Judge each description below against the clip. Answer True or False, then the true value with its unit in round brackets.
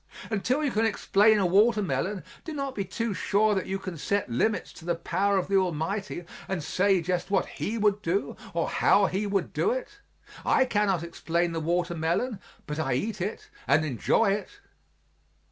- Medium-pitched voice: False (195 Hz)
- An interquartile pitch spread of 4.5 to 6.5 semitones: False (3.6 semitones)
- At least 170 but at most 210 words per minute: True (180 wpm)